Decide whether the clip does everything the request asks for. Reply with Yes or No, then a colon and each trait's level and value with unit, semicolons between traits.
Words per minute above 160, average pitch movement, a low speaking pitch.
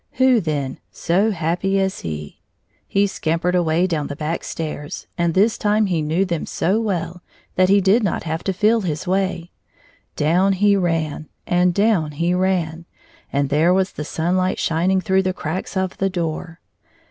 No: average, 180 wpm; average, 3.0 semitones; medium, 180 Hz